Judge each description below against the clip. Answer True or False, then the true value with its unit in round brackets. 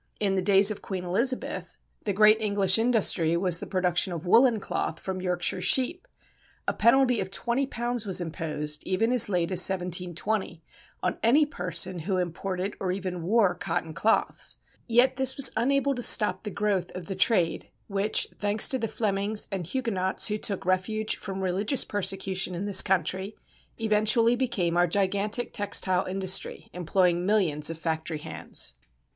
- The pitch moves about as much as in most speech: True (3.5 semitones)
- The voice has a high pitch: True (195 Hz)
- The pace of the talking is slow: False (160 wpm)